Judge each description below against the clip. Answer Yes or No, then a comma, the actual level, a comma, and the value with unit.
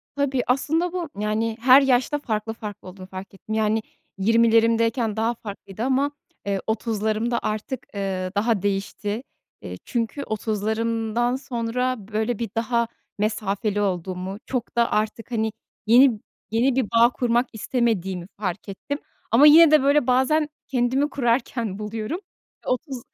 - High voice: Yes, high, 230 Hz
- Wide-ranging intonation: No, average, 3.1 semitones